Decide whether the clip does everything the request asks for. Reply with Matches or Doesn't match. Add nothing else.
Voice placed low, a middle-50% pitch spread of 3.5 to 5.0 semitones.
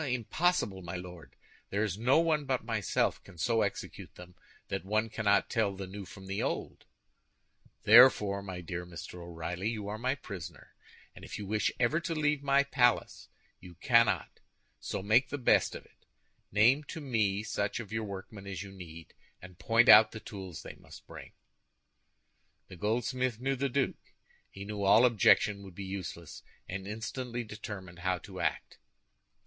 Matches